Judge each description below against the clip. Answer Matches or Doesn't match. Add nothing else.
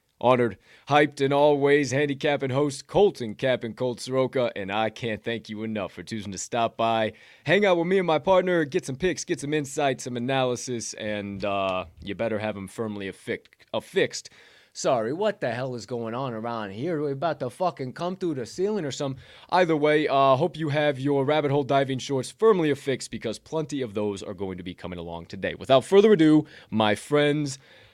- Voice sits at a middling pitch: Doesn't match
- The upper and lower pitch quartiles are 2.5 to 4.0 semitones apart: Doesn't match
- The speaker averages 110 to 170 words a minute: Doesn't match